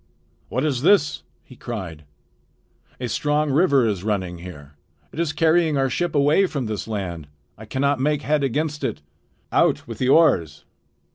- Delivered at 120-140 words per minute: No, average, 160 wpm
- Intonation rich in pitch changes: Yes, wide, 6.5 semitones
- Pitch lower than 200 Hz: Yes, low, 135 Hz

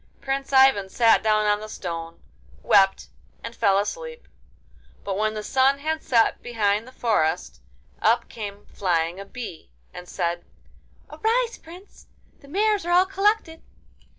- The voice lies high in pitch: Yes, high, 225 Hz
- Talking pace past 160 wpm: No, average, 145 wpm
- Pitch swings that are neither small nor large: No, wide, 8.2 semitones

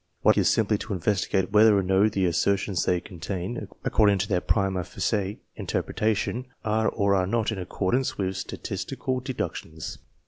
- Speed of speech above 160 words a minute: Yes, average, 170 wpm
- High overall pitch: No, low, 100 Hz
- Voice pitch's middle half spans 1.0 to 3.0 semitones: Yes, narrow, 2.6 semitones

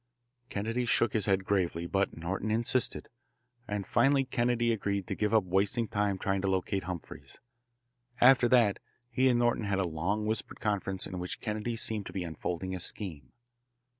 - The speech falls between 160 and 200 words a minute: Yes, average, 170 wpm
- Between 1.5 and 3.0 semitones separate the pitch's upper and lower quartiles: No, average, 3.5 semitones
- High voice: No, low, 100 Hz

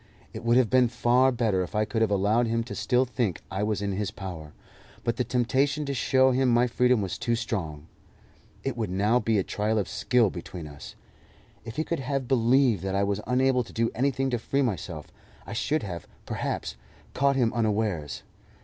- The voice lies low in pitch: Yes, low, 115 Hz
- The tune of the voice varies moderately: Yes, average, 4.0 semitones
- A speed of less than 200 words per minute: No, fast, 205 wpm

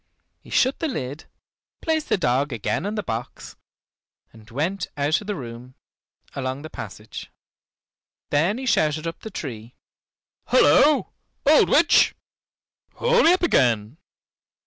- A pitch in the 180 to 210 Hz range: No, medium, 155 Hz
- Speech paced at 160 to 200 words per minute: No, slow, 135 wpm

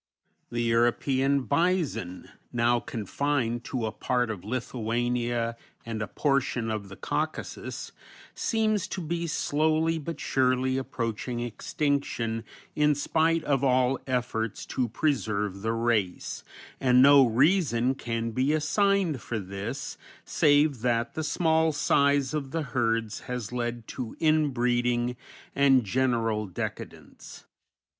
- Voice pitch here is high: No, low, 125 Hz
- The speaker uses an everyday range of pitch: Yes, average, 3.9 semitones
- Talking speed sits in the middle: No, slow, 120 wpm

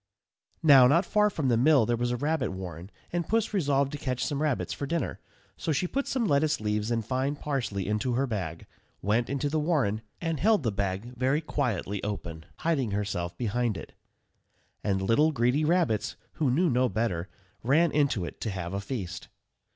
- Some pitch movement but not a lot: No, wide, 6.2 semitones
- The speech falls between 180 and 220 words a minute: Yes, average, 190 wpm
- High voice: No, low, 125 Hz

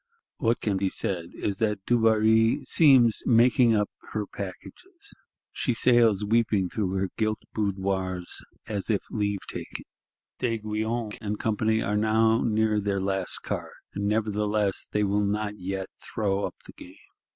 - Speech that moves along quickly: No, average, 140 wpm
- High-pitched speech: No, low, 105 Hz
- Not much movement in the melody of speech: Yes, narrow, 2.2 semitones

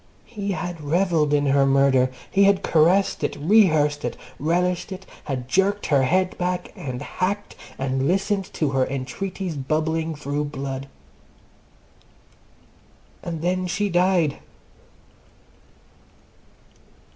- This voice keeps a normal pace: No, slow, 115 wpm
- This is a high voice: No, medium, 165 Hz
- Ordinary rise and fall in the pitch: Yes, average, 4.9 semitones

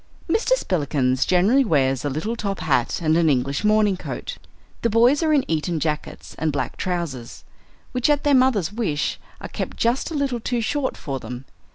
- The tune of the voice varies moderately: No, wide, 8.9 semitones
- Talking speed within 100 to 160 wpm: No, average, 185 wpm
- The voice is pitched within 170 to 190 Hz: Yes, medium, 185 Hz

